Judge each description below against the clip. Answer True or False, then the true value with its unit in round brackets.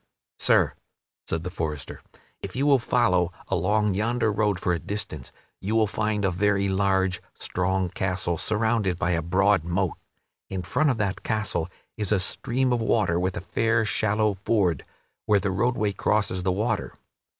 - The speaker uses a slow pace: False (165 wpm)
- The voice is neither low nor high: False (100 Hz)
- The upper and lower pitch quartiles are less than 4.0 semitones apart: True (3.0 semitones)